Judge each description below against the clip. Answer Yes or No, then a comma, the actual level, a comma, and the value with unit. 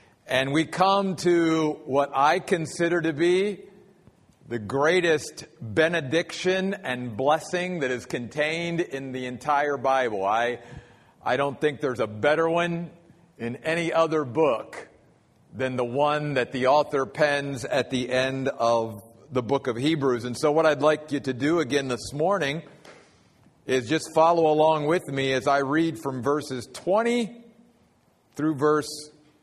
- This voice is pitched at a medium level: Yes, medium, 150 Hz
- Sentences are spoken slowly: No, average, 150 wpm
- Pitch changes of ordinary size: Yes, average, 3.8 semitones